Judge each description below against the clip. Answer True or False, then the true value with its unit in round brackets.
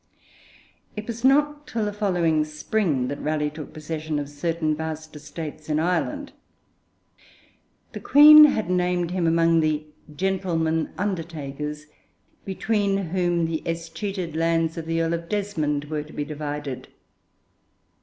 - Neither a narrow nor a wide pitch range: True (3.8 semitones)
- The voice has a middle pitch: True (165 Hz)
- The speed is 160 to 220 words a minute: False (135 wpm)